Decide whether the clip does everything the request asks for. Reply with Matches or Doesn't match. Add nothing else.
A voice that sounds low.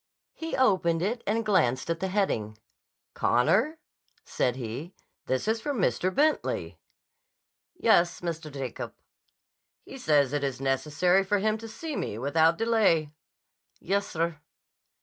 Doesn't match